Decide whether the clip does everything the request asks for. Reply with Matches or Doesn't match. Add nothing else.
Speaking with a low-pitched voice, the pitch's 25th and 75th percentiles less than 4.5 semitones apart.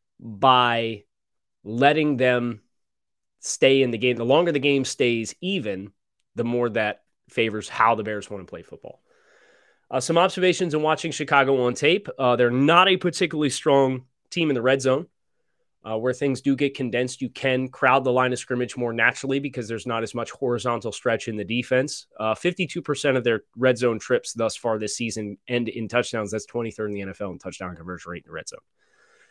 Matches